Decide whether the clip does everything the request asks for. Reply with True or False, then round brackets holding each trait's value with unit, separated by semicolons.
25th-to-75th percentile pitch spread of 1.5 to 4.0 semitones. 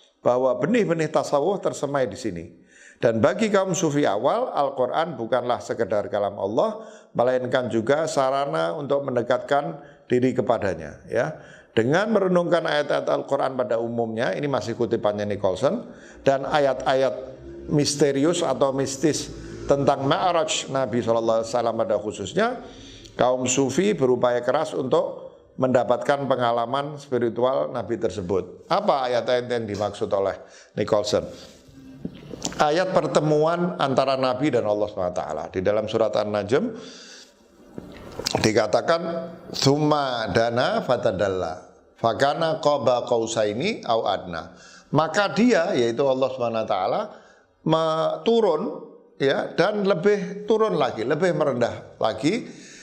False (5.5 semitones)